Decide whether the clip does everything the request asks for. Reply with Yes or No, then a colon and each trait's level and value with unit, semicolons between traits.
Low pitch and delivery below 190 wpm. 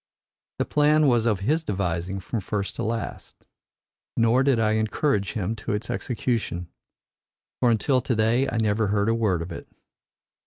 Yes: low, 110 Hz; average, 165 wpm